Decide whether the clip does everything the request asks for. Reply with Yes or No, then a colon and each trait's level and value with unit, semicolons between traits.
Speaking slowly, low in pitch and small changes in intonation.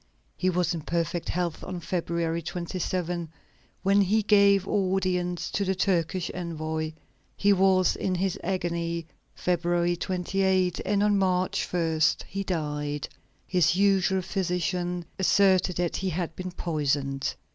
No: slow, 130 wpm; medium, 180 Hz; narrow, 2.0 semitones